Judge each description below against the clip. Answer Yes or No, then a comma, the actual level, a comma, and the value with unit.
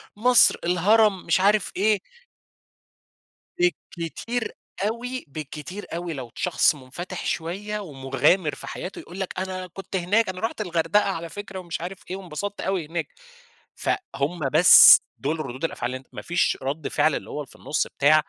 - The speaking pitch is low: No, medium, 180 Hz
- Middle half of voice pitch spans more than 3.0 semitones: Yes, average, 4.5 semitones